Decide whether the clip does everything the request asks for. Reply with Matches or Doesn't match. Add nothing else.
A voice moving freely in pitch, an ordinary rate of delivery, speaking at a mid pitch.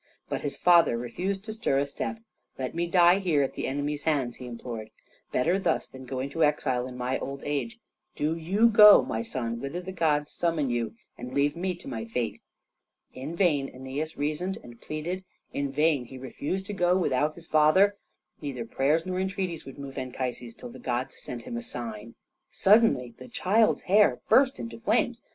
Matches